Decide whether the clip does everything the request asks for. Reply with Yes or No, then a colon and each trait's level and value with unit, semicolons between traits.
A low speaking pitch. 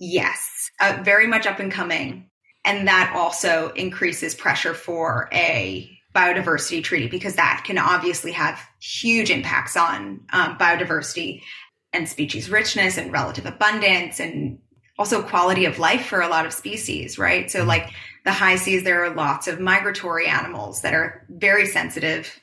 No: medium, 180 Hz